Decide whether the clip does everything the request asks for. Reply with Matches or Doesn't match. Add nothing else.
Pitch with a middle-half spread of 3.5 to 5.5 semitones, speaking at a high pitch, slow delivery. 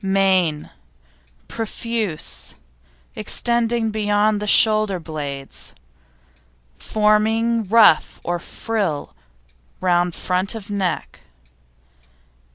Matches